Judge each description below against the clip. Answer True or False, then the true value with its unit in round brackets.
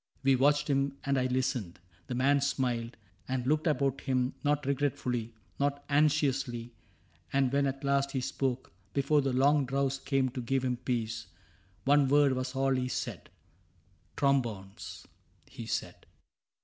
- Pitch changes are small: True (1.8 semitones)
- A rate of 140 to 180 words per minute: True (155 wpm)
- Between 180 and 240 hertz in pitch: False (135 Hz)